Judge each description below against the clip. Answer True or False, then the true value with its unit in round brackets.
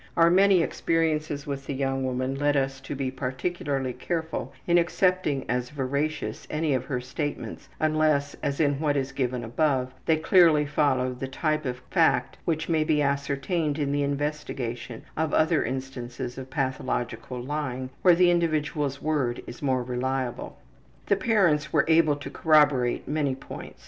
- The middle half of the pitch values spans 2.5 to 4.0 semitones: True (3.0 semitones)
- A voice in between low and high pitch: True (145 Hz)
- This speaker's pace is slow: False (160 wpm)